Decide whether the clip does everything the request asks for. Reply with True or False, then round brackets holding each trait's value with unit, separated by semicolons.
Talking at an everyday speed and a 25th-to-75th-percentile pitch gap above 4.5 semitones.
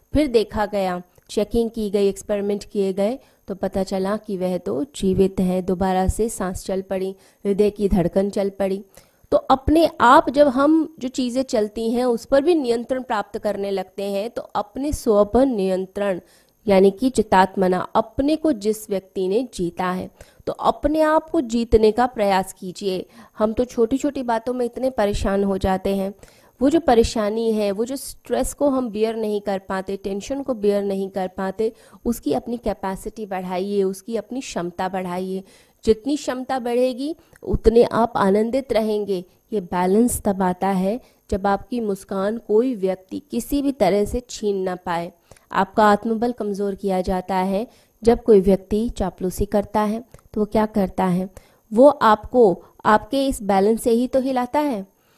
False (170 wpm; 3.8 semitones)